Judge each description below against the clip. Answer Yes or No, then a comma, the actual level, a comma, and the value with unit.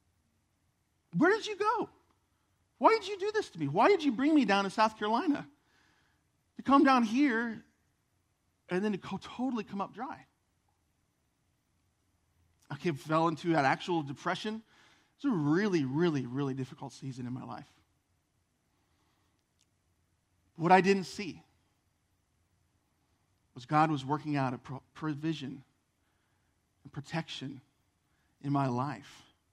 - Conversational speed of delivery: No, slow, 130 wpm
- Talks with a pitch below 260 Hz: Yes, medium, 140 Hz